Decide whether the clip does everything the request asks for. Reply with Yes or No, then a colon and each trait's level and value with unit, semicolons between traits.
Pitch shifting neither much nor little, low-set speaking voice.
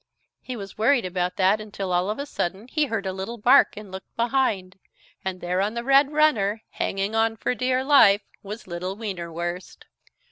No: average, 4.3 semitones; high, 205 Hz